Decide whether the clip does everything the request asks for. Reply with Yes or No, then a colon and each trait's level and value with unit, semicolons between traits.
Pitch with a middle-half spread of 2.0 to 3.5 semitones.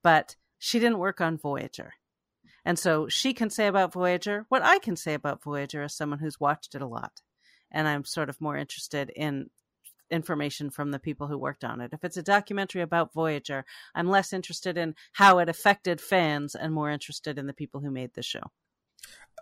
No: average, 4.0 semitones